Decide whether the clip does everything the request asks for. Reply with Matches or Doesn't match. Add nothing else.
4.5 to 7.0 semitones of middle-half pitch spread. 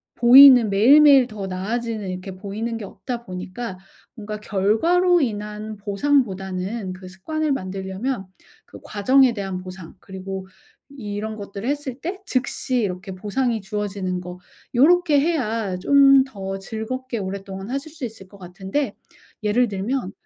Matches